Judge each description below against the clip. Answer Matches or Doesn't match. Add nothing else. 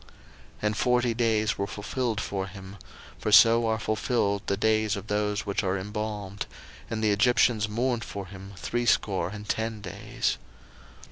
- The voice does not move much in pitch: Matches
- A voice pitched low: Matches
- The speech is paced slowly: Doesn't match